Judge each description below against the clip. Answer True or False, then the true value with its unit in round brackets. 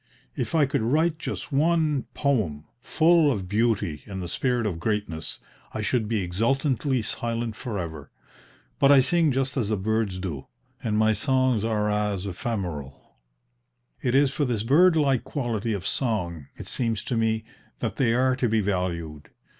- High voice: False (115 Hz)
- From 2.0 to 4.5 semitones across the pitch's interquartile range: False (5.2 semitones)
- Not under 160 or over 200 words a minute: True (170 wpm)